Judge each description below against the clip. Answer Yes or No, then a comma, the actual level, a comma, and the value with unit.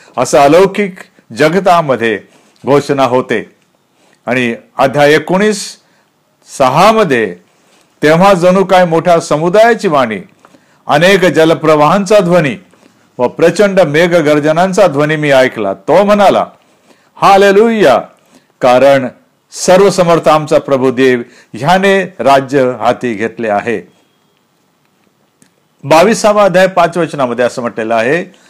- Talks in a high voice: No, medium, 160 Hz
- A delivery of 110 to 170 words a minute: No, average, 95 wpm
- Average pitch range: No, wide, 6.1 semitones